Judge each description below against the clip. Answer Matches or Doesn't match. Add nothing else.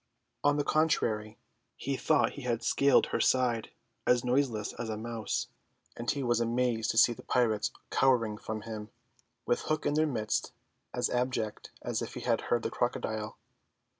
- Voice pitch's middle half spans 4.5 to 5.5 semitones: Doesn't match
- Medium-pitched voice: Doesn't match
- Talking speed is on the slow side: Doesn't match